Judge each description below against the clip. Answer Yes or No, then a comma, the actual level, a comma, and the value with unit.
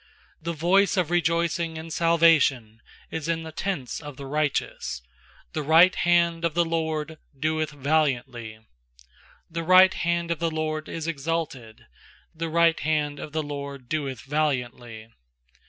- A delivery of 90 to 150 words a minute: Yes, average, 140 wpm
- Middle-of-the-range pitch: Yes, medium, 155 Hz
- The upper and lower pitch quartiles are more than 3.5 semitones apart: No, average, 2.9 semitones